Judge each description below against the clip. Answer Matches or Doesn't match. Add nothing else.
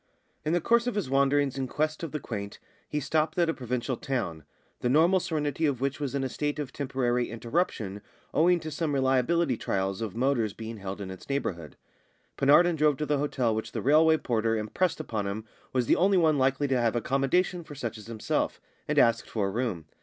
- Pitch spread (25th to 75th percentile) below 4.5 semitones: Doesn't match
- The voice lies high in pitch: Doesn't match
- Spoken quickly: Matches